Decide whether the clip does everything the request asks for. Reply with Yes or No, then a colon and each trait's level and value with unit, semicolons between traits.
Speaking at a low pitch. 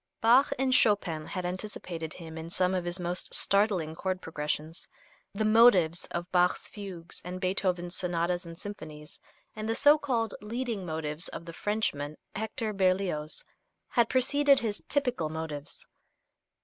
No: medium, 185 Hz